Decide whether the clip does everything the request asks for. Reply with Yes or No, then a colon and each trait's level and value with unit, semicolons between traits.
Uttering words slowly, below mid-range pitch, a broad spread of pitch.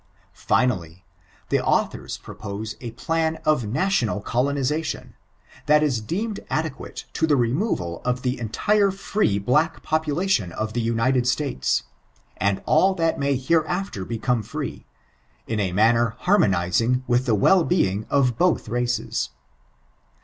Yes: slow, 125 wpm; low, 125 Hz; wide, 6.4 semitones